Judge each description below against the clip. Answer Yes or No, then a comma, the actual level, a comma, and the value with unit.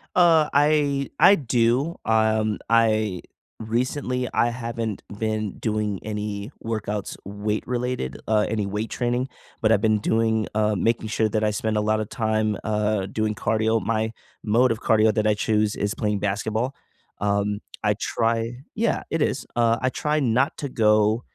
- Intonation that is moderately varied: No, narrow, 2.0 semitones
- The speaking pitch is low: Yes, low, 110 Hz